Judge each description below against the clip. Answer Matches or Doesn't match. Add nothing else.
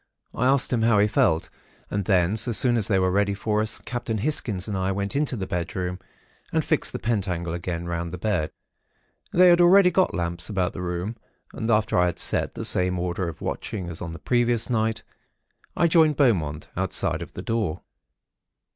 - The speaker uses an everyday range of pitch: Matches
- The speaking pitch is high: Doesn't match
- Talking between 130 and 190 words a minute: Doesn't match